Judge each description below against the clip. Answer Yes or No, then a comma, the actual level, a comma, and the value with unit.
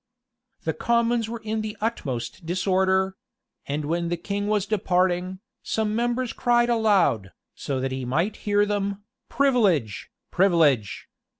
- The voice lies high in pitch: Yes, high, 200 Hz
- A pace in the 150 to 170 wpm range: No, slow, 135 wpm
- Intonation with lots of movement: No, average, 5.0 semitones